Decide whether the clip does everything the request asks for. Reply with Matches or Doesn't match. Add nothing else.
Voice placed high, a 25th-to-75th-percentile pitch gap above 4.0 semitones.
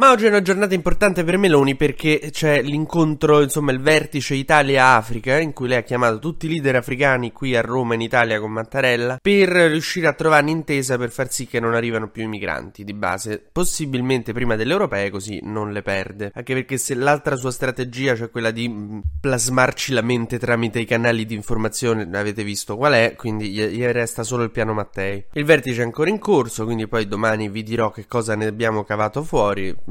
Doesn't match